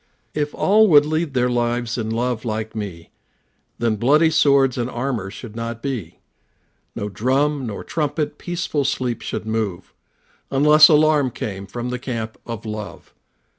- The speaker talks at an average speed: Yes, average, 150 wpm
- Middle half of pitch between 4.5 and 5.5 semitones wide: Yes, average, 4.8 semitones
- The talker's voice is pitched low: Yes, low, 125 Hz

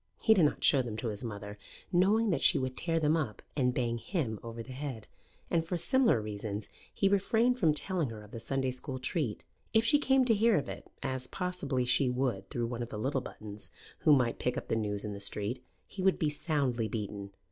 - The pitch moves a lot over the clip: Yes, wide, 7.1 semitones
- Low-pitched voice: Yes, low, 130 Hz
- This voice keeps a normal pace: No, fast, 225 wpm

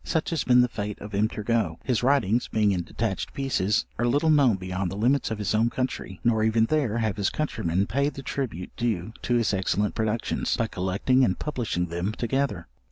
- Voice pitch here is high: No, low, 110 Hz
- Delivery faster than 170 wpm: Yes, fast, 205 wpm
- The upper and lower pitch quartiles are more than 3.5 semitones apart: Yes, average, 4.2 semitones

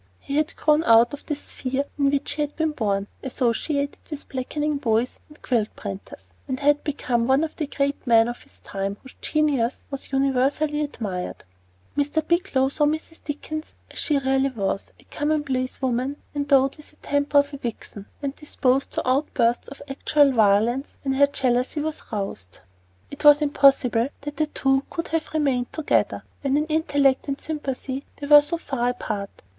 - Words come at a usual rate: Yes, average, 175 wpm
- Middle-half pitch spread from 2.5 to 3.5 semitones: Yes, average, 2.9 semitones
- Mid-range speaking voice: No, very high, 275 Hz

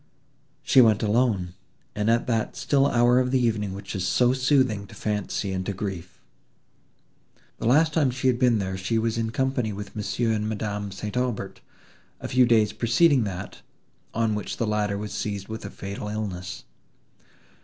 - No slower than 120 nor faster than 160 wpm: No, average, 175 wpm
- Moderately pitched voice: No, low, 110 Hz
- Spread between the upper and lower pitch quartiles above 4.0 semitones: No, average, 3.3 semitones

